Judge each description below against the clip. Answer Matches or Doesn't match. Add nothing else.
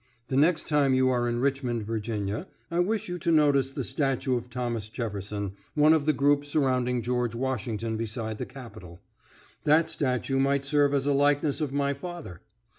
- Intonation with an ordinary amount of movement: Matches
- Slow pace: Doesn't match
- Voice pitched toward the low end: Matches